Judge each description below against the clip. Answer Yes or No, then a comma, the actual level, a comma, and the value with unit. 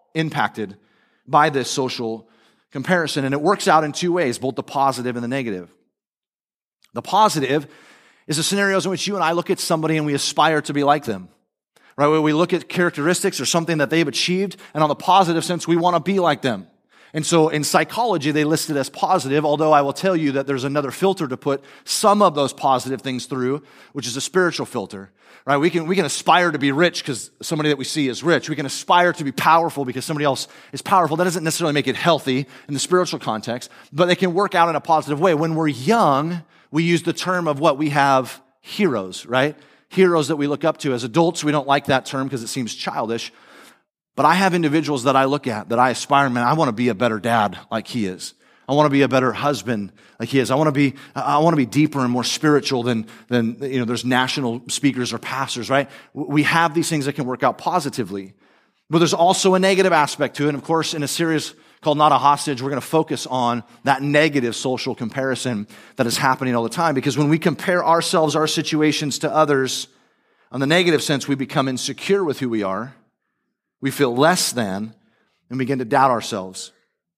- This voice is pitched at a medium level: Yes, medium, 145 Hz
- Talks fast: Yes, fast, 230 wpm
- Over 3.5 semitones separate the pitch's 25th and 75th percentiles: Yes, average, 4.0 semitones